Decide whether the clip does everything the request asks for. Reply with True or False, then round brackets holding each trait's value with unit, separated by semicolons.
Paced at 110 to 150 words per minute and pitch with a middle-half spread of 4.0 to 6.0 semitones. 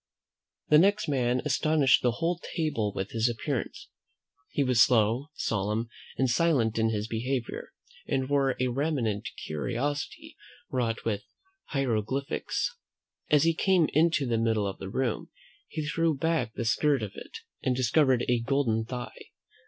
True (145 wpm; 4.5 semitones)